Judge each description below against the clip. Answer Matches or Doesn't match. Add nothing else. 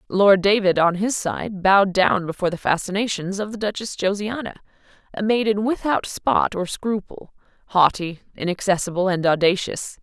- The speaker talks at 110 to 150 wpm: Matches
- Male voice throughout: Doesn't match